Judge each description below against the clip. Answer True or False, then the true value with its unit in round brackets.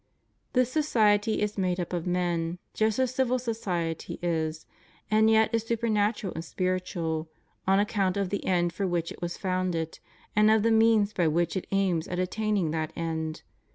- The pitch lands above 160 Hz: True (190 Hz)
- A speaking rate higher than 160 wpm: True (180 wpm)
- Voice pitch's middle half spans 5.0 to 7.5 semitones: False (4.0 semitones)